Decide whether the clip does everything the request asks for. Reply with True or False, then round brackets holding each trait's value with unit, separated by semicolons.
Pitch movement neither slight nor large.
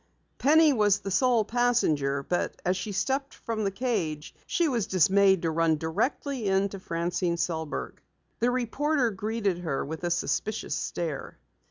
False (6.2 semitones)